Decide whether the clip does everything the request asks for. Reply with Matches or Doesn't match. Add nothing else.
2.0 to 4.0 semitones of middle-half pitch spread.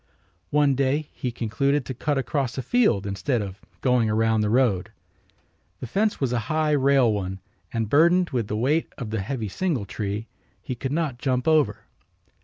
Doesn't match